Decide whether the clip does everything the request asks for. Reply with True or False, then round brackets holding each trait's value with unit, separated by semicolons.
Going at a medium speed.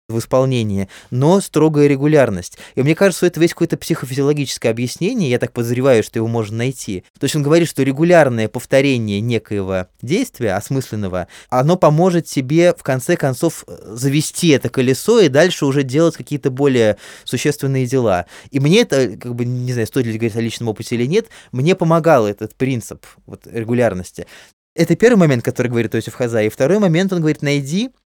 False (175 wpm)